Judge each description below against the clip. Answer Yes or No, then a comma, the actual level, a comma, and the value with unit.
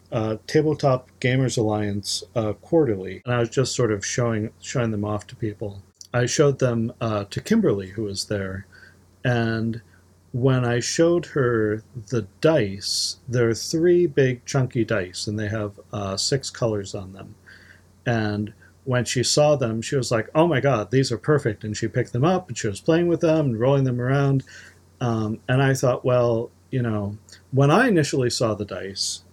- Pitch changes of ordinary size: Yes, average, 4.3 semitones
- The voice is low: Yes, low, 115 Hz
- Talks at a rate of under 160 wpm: No, average, 180 wpm